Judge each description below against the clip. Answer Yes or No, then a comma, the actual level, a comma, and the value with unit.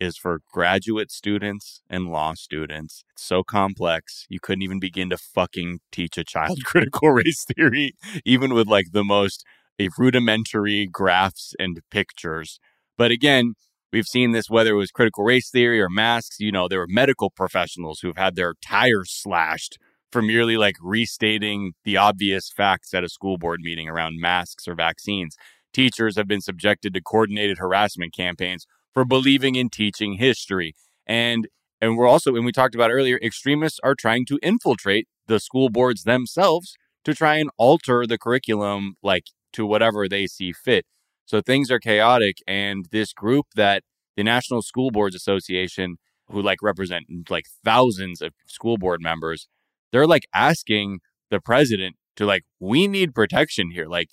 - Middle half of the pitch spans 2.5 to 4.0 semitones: No, average, 4.4 semitones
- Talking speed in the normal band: Yes, average, 165 wpm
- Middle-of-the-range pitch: No, low, 105 Hz